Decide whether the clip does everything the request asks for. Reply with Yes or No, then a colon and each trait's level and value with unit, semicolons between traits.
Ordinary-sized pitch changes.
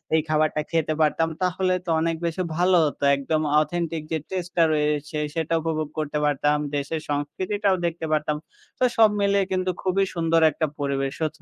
Yes: average, 3.1 semitones